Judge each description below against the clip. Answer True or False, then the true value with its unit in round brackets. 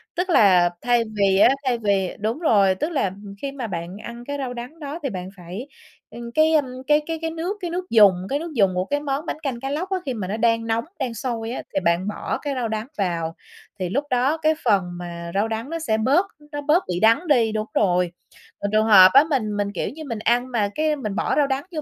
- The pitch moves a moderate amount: False (6.3 semitones)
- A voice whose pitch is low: False (235 Hz)